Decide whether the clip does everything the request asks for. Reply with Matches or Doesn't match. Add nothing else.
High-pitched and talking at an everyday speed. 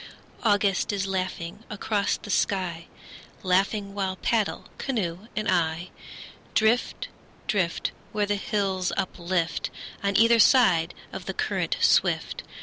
Doesn't match